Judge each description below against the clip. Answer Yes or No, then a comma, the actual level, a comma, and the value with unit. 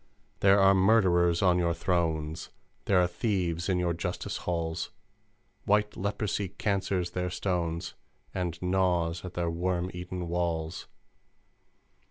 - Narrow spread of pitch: Yes, narrow, 1.8 semitones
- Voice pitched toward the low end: Yes, very low, 90 Hz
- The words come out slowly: Yes, slow, 125 wpm